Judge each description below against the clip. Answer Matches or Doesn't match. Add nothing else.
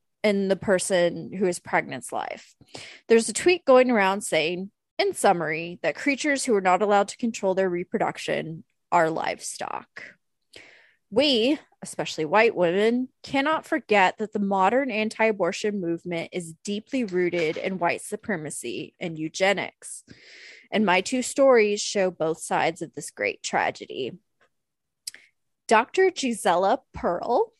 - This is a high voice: Matches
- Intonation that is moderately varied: Doesn't match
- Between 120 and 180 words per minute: Matches